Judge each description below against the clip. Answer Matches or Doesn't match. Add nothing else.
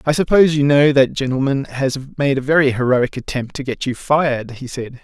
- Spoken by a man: Matches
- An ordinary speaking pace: Doesn't match